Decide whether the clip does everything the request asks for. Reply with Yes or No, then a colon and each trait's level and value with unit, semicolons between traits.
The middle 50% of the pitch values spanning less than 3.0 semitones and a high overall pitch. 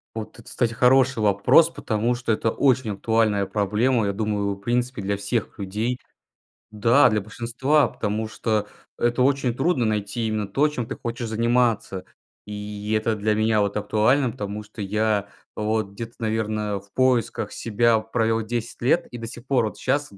No: narrow, 2.4 semitones; low, 110 Hz